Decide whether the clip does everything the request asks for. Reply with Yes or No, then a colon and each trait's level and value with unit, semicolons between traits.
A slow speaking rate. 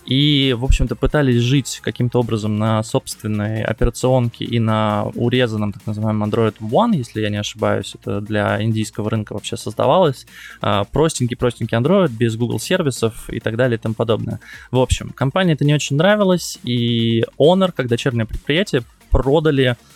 No: average, 155 wpm